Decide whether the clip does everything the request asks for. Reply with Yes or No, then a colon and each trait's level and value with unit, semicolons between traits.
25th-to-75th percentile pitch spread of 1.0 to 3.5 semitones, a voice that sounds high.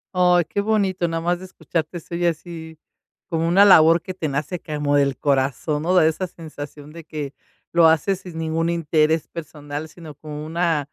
No: narrow, 2.4 semitones; medium, 165 Hz